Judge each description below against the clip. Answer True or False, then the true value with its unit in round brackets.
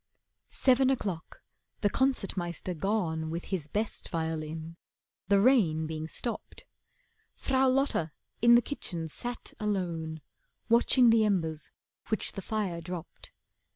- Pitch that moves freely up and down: True (6.4 semitones)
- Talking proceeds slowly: True (120 wpm)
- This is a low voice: False (190 Hz)